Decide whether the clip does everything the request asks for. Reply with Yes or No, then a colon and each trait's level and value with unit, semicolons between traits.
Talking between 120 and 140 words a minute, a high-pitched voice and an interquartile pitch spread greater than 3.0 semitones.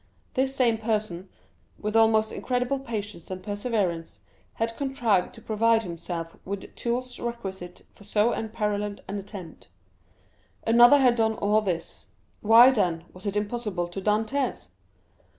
Yes: slow, 135 wpm; high, 215 Hz; average, 3.4 semitones